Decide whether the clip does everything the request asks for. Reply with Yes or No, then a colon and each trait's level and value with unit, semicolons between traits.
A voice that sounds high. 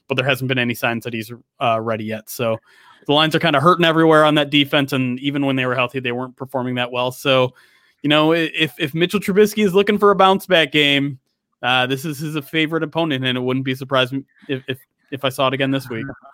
No: low, 135 Hz